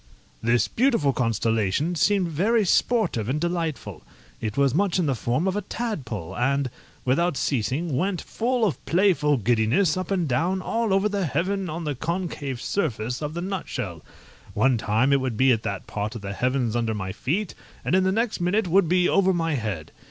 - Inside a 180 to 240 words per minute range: Yes, average, 190 wpm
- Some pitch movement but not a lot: No, wide, 7.5 semitones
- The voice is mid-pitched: Yes, medium, 150 Hz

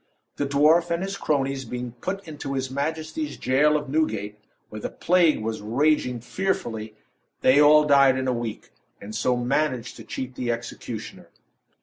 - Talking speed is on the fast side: No, average, 160 wpm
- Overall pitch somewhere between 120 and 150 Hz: Yes, low, 135 Hz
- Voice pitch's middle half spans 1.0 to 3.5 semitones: No, average, 4.1 semitones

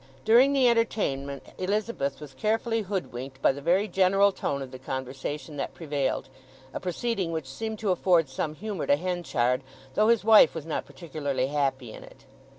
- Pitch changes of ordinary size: No, wide, 7.3 semitones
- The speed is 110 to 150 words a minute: No, average, 165 wpm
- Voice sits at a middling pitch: Yes, medium, 160 Hz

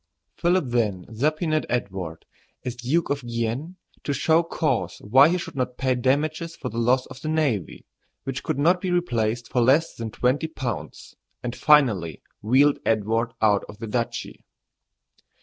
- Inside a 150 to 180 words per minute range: Yes, average, 160 wpm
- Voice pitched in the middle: No, low, 130 Hz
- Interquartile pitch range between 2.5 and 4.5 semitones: No, average, 5.2 semitones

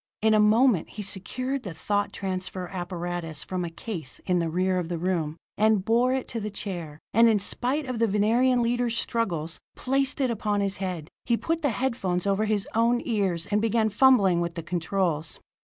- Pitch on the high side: Yes, high, 205 Hz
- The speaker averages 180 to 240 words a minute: Yes, average, 200 wpm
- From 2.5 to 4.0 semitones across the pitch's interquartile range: No, average, 4.7 semitones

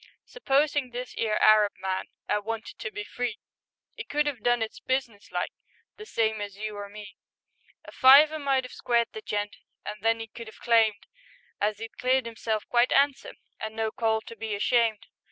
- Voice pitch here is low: No, high, 225 Hz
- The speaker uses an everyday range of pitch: Yes, average, 3.2 semitones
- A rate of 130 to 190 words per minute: Yes, average, 185 wpm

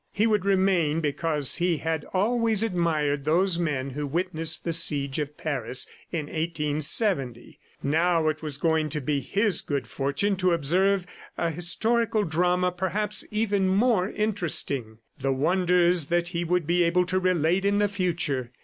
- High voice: No, medium, 170 Hz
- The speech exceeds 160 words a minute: No, average, 155 wpm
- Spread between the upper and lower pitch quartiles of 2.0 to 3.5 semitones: No, average, 4.0 semitones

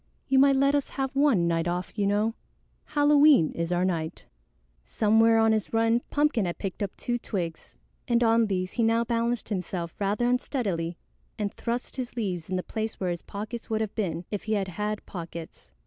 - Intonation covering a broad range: No, average, 4.6 semitones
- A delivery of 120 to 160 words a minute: No, average, 195 wpm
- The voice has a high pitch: Yes, high, 215 Hz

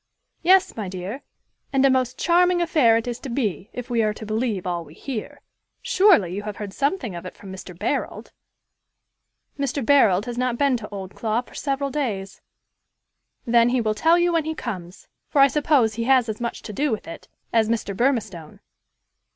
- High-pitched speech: Yes, high, 235 Hz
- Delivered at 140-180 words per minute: No, average, 190 wpm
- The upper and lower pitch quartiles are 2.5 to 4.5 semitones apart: No, average, 5.1 semitones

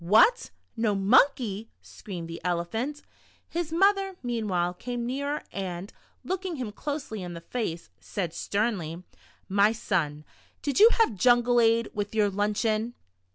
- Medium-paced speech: Yes, average, 145 wpm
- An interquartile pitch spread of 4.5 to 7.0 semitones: Yes, average, 5.2 semitones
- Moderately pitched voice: No, high, 220 Hz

